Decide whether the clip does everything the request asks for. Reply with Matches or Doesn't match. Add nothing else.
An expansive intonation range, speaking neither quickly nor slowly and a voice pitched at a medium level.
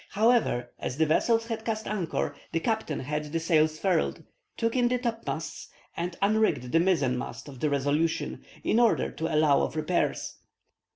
Matches